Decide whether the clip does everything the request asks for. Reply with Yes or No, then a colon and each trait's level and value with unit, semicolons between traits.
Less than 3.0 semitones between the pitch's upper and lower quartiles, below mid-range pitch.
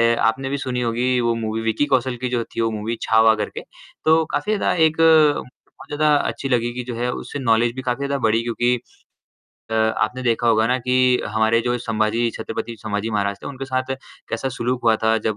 Yes: narrow, 2.6 semitones; low, 120 Hz